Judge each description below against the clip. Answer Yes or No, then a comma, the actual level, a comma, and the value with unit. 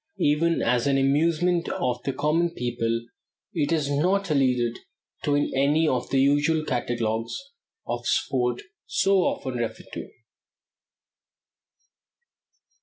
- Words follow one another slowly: Yes, slow, 115 wpm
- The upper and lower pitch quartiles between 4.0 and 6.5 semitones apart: Yes, average, 4.6 semitones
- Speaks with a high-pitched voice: No, medium, 140 Hz